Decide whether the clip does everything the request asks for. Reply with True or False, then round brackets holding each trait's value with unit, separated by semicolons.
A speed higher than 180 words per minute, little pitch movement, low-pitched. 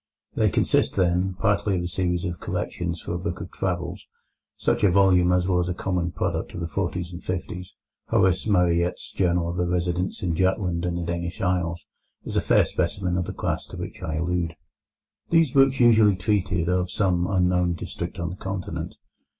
True (190 wpm; 1.4 semitones; 90 Hz)